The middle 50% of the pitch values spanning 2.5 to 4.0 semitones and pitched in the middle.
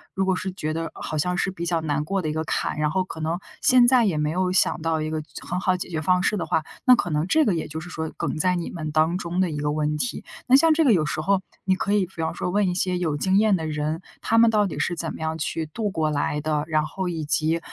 Yes: average, 3.4 semitones; medium, 170 Hz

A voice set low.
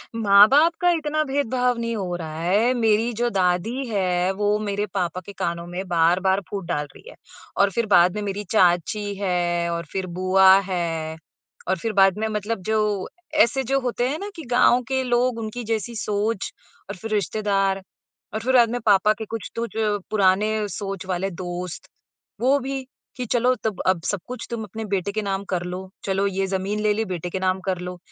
No: high, 205 Hz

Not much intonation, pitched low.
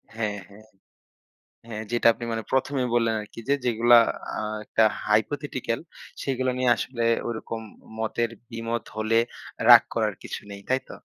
Yes: narrow, 1.7 semitones; low, 115 Hz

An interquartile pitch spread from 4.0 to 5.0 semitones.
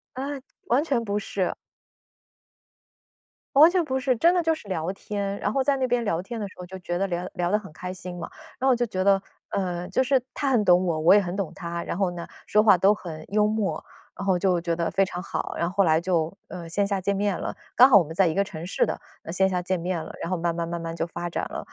No: average, 3.4 semitones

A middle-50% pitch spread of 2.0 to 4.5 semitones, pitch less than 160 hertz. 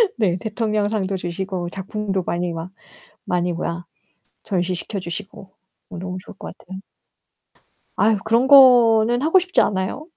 No: average, 3.7 semitones; high, 195 Hz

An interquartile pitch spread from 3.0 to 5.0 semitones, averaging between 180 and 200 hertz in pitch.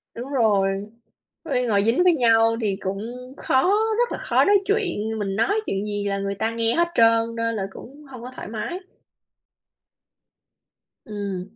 No: average, 4.4 semitones; high, 225 Hz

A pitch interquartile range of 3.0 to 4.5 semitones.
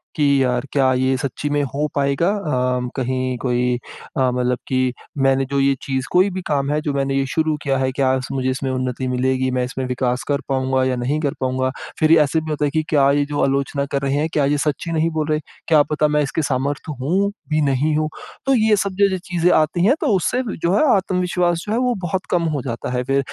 Yes: average, 3.3 semitones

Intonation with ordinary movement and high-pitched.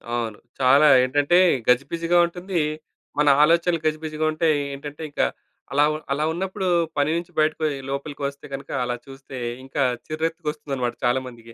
No: average, 3.1 semitones; medium, 150 Hz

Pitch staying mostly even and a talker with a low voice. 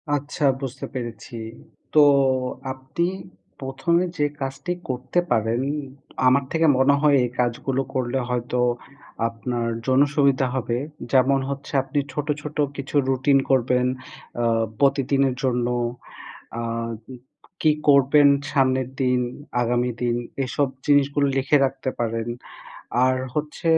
Yes: narrow, 2.3 semitones; low, 130 Hz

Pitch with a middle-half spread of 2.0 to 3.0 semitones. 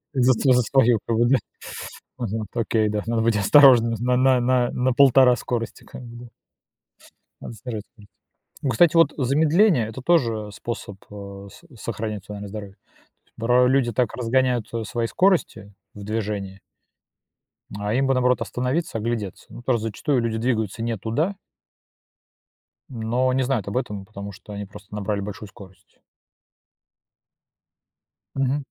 No: average, 3.4 semitones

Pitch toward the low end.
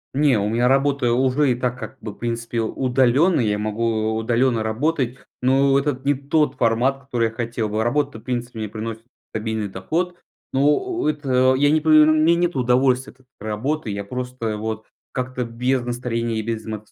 Yes: low, 125 Hz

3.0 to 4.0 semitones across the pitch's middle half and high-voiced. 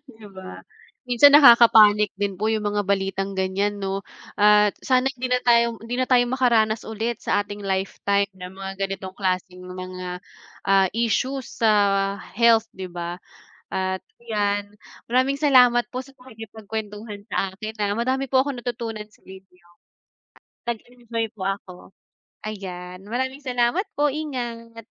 Yes: average, 3.7 semitones; high, 215 Hz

